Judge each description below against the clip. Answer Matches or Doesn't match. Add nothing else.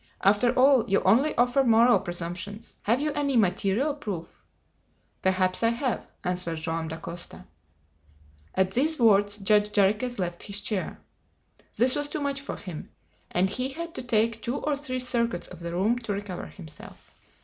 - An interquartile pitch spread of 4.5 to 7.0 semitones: Matches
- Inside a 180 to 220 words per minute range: Doesn't match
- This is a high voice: Matches